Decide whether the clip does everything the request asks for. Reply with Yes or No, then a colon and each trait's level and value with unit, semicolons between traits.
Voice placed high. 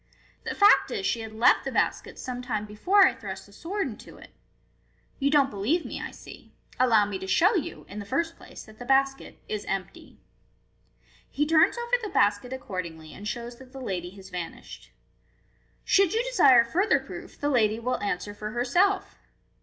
Yes: high, 245 Hz